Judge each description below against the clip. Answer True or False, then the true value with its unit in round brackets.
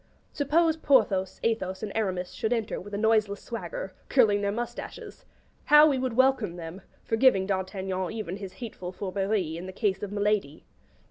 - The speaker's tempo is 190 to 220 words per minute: False (160 wpm)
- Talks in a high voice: True (205 Hz)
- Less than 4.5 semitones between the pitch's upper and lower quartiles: True (3.4 semitones)